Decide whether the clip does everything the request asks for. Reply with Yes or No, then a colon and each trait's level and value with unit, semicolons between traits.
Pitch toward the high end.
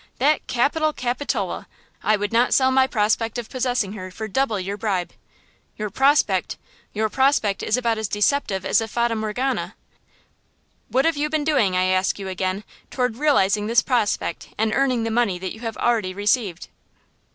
Yes: high, 225 Hz